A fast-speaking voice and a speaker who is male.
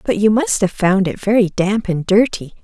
No: fast, 230 wpm; female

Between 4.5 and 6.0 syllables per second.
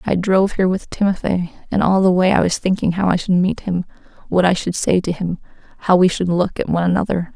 No: 6.2 syllables/s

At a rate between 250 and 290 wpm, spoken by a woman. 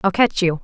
Yes: fast, 285 wpm; female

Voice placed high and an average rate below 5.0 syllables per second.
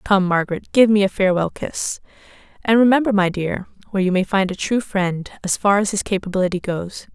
No: high, 195 Hz; 5.9 syllables/s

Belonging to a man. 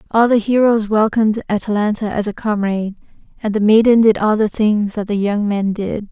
No: female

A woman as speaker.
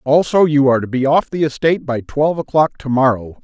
No: male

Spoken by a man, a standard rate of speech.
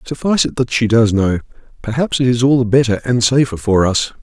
No: male; fast, 215 wpm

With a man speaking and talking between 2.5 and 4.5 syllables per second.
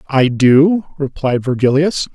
Yes: male; 3.8 syllables/s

